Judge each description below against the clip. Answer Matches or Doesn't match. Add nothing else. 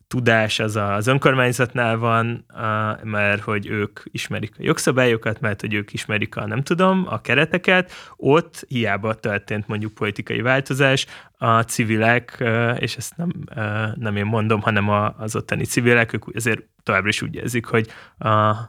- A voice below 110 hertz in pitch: Doesn't match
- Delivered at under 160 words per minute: Matches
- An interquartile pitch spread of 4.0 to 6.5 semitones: Doesn't match